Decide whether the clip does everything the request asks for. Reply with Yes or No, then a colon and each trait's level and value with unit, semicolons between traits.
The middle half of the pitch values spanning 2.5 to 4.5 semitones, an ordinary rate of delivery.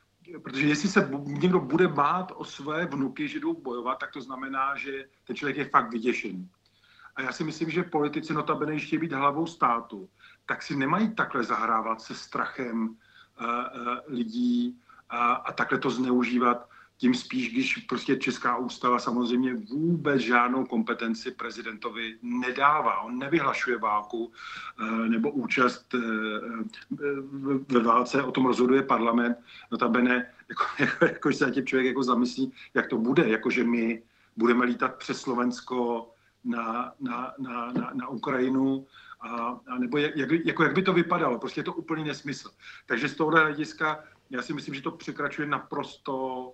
Yes: average, 4.0 semitones; average, 155 wpm